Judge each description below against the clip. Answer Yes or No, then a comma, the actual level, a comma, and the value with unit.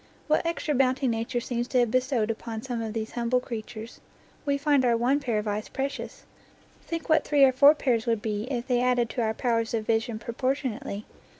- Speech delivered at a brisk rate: Yes, fast, 210 wpm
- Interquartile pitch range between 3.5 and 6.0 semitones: No, average, 3.0 semitones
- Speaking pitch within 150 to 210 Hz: No, high, 240 Hz